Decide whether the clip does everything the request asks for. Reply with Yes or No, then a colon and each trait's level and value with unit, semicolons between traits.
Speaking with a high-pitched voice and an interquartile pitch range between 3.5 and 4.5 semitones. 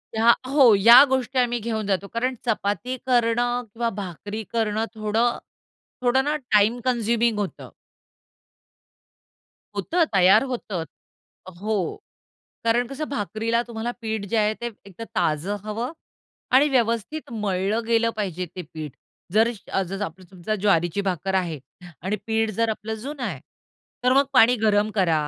No: high, 220 Hz; average, 3.1 semitones